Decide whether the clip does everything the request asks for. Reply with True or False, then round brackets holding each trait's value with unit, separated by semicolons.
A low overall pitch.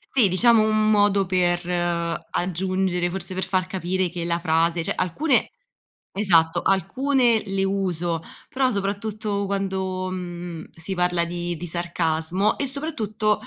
False (185 Hz)